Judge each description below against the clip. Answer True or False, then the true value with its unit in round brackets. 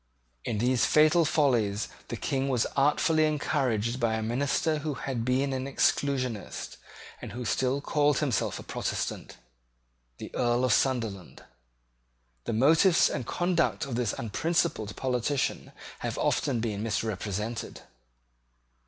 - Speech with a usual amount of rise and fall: True (4.2 semitones)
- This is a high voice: False (130 Hz)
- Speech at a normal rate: False (125 wpm)